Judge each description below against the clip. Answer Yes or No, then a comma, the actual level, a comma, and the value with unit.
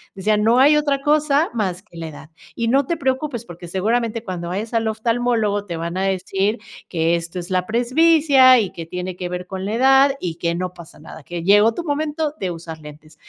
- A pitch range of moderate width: No, wide, 6.5 semitones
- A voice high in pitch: Yes, high, 210 Hz